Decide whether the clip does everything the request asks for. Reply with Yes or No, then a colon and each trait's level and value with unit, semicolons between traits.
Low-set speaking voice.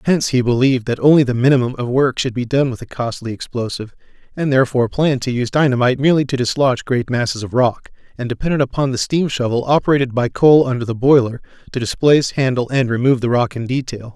Yes: low, 130 Hz